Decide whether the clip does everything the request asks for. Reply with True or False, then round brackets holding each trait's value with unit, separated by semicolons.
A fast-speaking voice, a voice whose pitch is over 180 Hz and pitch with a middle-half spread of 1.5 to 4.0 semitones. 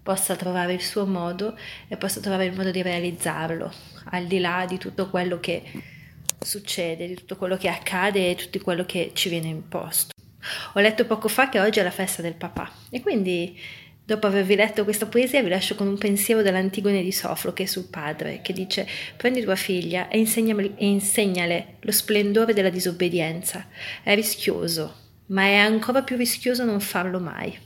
True (180 wpm; 190 Hz; 2.8 semitones)